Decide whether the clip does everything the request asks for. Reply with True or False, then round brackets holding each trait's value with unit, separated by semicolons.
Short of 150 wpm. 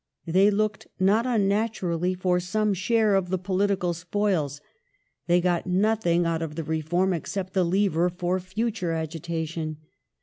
True (135 wpm)